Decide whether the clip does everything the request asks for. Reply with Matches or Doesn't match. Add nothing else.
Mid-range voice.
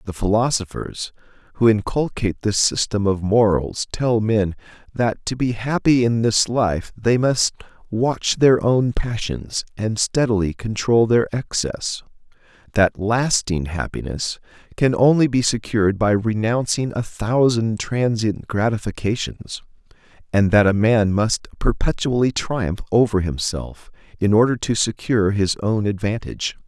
Doesn't match